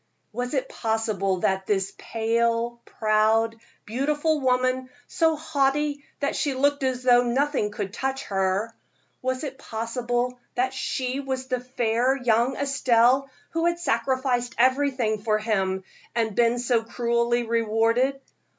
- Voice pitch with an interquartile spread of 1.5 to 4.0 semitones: Yes, average, 2.9 semitones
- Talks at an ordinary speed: No, slow, 130 wpm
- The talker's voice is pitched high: Yes, high, 245 Hz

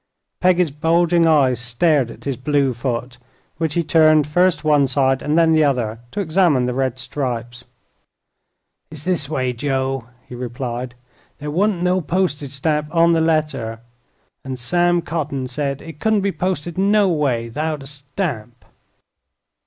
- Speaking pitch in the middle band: Yes, medium, 150 Hz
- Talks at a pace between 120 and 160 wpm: Yes, average, 155 wpm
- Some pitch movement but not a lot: Yes, average, 4.5 semitones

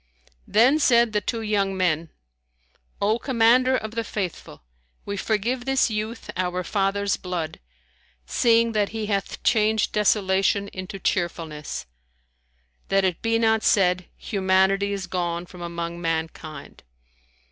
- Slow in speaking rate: Yes, slow, 125 wpm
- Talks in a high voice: Yes, high, 200 Hz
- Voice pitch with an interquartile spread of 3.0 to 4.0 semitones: Yes, average, 3.6 semitones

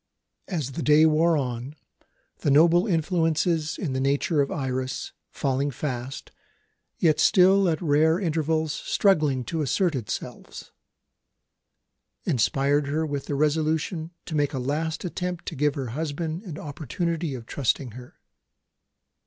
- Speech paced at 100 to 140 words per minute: Yes, slow, 135 wpm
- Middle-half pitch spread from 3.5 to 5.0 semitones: No, average, 2.9 semitones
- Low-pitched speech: No, medium, 150 Hz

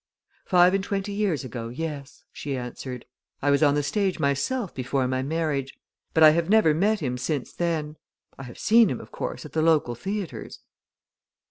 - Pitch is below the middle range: No, medium, 150 Hz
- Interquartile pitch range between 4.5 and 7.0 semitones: Yes, average, 5.3 semitones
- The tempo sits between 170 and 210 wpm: Yes, average, 185 wpm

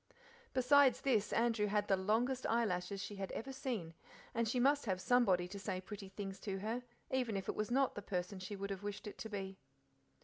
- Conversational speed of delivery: No, fast, 210 wpm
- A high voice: Yes, high, 210 Hz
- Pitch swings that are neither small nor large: Yes, average, 3.8 semitones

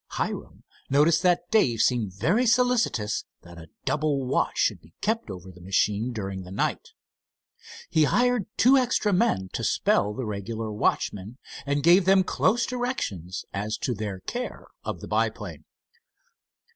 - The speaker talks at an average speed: Yes, average, 150 wpm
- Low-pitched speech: Yes, low, 115 Hz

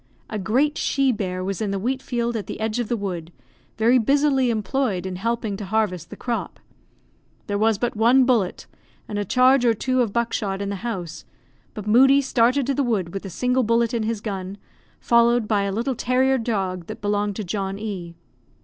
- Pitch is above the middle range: Yes, high, 220 Hz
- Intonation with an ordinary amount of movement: Yes, average, 3.8 semitones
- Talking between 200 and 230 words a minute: Yes, fast, 205 wpm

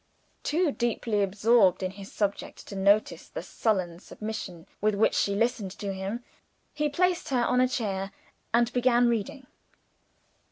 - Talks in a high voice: Yes, high, 215 Hz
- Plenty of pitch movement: No, average, 3.8 semitones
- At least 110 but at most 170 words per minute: Yes, average, 150 wpm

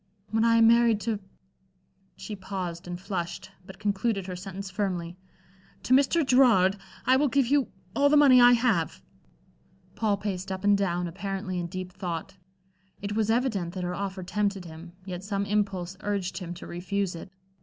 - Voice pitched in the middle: No, high, 195 Hz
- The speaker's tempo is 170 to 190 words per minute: Yes, average, 175 wpm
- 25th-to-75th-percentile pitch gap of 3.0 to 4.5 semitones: Yes, average, 3.6 semitones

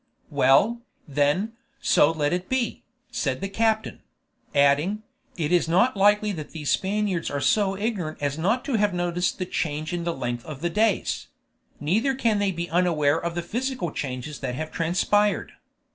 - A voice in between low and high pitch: Yes, medium, 175 Hz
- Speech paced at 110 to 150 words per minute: No, average, 170 wpm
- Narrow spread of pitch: No, wide, 5.6 semitones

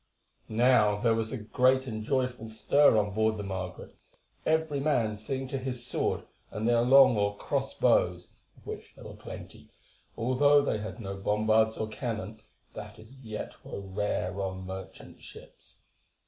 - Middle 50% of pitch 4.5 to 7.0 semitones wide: No, average, 3.7 semitones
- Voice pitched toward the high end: No, low, 110 Hz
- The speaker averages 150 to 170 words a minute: Yes, average, 160 wpm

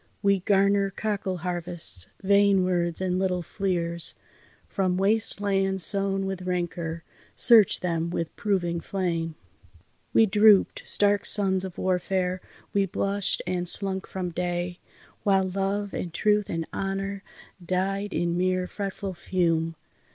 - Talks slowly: Yes, slow, 130 wpm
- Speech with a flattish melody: Yes, narrow, 2.1 semitones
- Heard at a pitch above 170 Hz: Yes, high, 190 Hz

